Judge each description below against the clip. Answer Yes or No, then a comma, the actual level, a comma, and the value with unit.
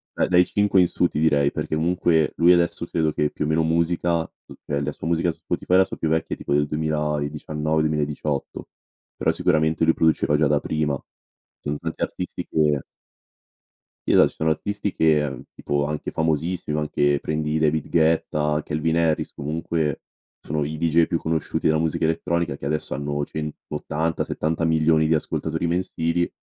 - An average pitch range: No, narrow, 1.5 semitones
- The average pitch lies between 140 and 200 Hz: No, very low, 80 Hz